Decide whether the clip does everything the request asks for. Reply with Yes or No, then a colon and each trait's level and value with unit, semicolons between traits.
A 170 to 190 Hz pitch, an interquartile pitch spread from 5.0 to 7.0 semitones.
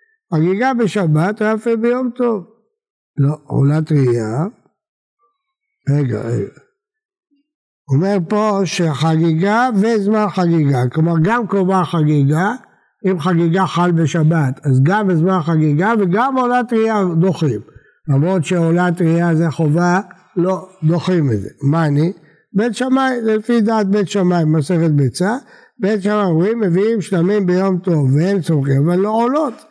Yes: medium, 185 Hz; wide, 5.4 semitones